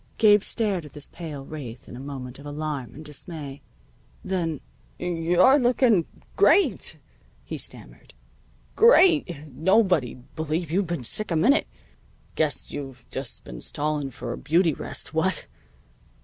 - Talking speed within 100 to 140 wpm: Yes, slow, 135 wpm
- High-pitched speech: No, medium, 155 Hz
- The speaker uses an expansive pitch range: No, average, 4.9 semitones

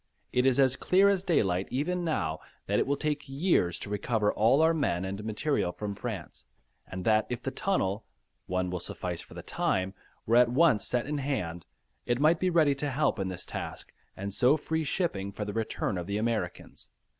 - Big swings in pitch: Yes, wide, 7.0 semitones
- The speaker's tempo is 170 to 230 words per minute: Yes, average, 200 wpm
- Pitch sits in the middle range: No, low, 120 Hz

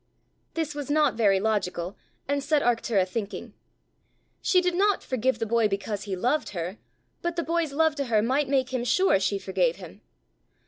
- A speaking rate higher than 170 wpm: Yes, average, 180 wpm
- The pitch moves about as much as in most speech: No, wide, 6.8 semitones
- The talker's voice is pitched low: No, high, 245 Hz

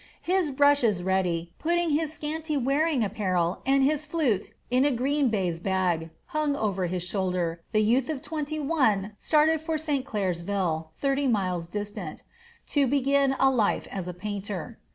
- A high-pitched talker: Yes, high, 240 Hz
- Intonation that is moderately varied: No, wide, 7.5 semitones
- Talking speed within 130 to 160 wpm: Yes, average, 155 wpm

